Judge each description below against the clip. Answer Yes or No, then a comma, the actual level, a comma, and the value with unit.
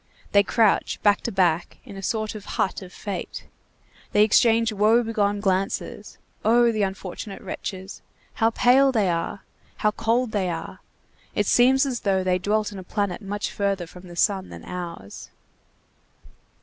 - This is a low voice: No, high, 205 Hz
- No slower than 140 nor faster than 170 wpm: Yes, average, 160 wpm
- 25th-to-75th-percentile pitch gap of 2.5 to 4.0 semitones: Yes, average, 2.9 semitones